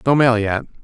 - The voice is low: Yes, low, 120 Hz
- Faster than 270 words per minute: No, fast, 215 wpm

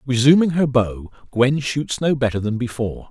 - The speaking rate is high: No, average, 175 wpm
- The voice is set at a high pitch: No, low, 130 Hz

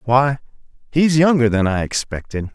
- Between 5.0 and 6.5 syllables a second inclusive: No, 4.7 syllables/s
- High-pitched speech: No, low, 125 Hz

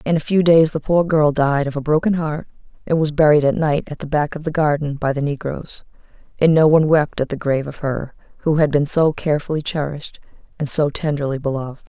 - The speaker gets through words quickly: Yes, fast, 225 wpm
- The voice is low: No, medium, 150 Hz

